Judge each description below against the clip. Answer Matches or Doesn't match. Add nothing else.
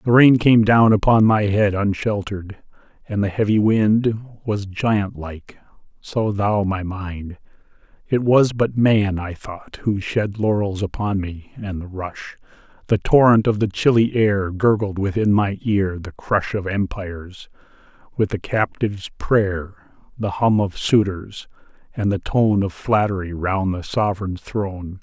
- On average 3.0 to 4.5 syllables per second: Matches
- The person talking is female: Doesn't match